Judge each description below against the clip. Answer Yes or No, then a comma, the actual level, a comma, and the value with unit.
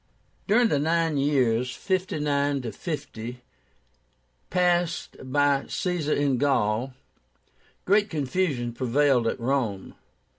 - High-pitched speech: No, medium, 140 Hz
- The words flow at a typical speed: No, slow, 90 wpm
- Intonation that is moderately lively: Yes, average, 5.0 semitones